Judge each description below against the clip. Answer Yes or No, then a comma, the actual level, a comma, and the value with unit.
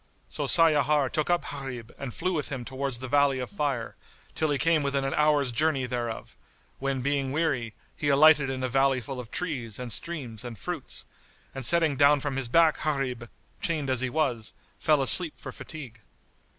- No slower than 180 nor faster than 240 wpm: Yes, average, 190 wpm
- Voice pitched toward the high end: No, low, 135 Hz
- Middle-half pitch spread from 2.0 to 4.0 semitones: Yes, average, 3.1 semitones